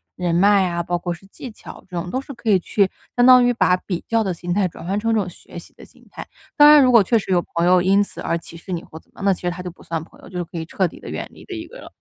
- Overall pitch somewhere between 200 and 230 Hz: No, medium, 185 Hz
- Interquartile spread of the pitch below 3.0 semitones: No, average, 4.2 semitones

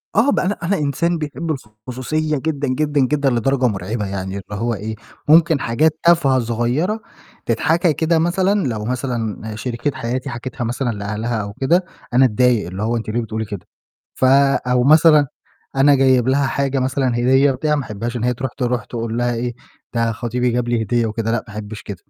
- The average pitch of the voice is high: No, low, 125 Hz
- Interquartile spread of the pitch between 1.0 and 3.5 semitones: No, average, 4.1 semitones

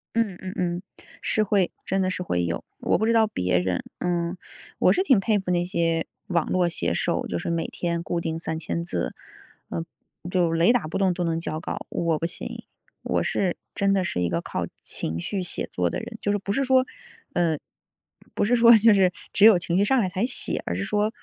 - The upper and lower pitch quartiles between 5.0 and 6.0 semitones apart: No, average, 3.7 semitones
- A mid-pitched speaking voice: Yes, medium, 180 Hz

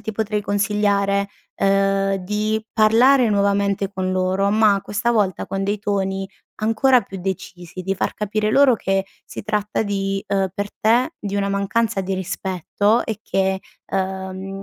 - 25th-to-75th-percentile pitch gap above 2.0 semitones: No, narrow, 1.7 semitones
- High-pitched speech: Yes, high, 200 Hz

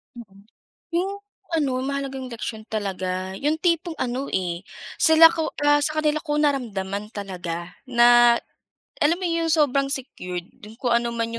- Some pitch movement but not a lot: No, wide, 6.8 semitones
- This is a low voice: No, very high, 250 Hz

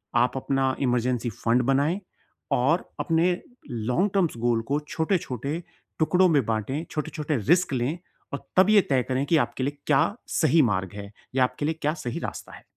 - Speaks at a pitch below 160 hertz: Yes, medium, 140 Hz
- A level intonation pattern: No, average, 4.7 semitones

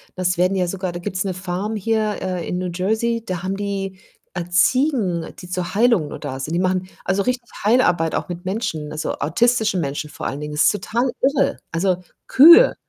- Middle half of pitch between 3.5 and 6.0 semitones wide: Yes, average, 3.9 semitones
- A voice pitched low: No, medium, 185 Hz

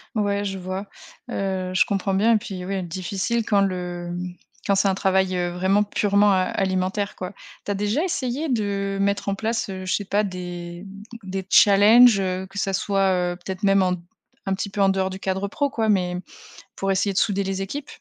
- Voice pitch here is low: No, high, 195 Hz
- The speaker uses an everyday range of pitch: No, narrow, 1.5 semitones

